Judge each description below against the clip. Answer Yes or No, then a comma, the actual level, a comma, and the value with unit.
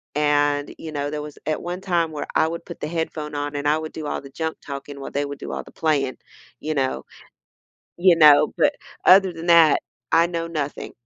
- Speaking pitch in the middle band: Yes, medium, 155 Hz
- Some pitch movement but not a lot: No, narrow, 2.3 semitones